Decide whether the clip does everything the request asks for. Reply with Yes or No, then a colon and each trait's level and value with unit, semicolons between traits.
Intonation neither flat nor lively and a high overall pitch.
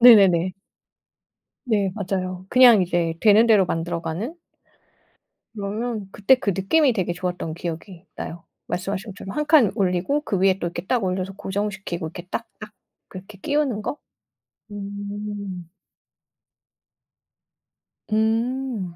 Yes: average, 3.4 semitones; high, 200 Hz